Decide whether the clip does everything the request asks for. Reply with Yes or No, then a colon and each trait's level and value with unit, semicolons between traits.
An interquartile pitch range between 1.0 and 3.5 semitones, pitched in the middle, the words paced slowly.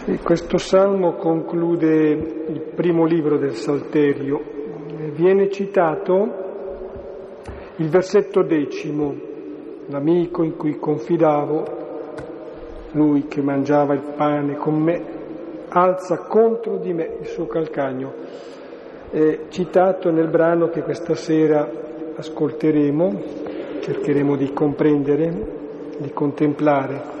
Yes: narrow, 2.6 semitones; medium, 155 Hz; slow, 95 wpm